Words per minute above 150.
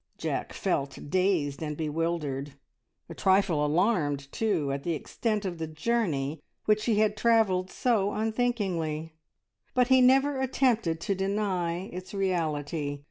No: slow, 135 wpm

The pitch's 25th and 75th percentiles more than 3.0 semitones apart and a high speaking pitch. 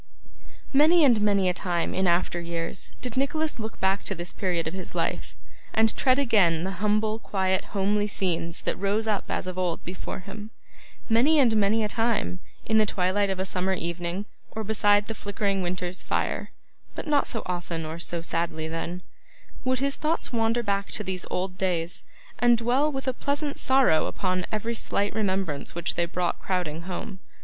Yes: average, 4.0 semitones; high, 195 Hz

